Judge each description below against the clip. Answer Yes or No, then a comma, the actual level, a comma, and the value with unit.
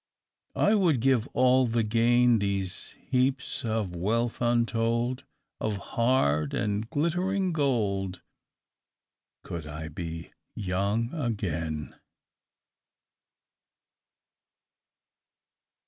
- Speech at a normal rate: No, slow, 80 wpm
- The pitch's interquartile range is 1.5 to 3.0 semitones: No, average, 4.7 semitones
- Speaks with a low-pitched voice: Yes, low, 115 Hz